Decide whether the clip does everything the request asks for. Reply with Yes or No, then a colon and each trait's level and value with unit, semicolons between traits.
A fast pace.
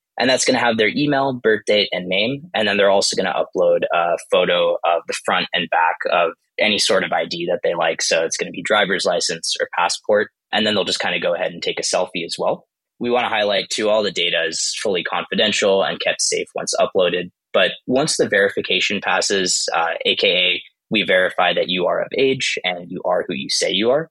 Yes: fast, 235 wpm